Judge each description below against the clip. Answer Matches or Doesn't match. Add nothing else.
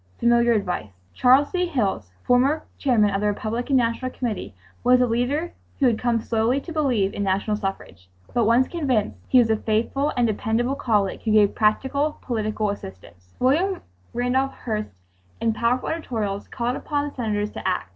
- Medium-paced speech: Matches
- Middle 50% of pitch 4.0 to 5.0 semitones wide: Doesn't match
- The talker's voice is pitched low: Doesn't match